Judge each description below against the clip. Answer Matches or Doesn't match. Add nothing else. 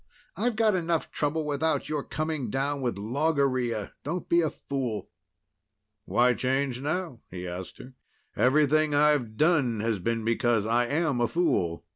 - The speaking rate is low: Doesn't match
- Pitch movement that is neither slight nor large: Matches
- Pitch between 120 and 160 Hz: Matches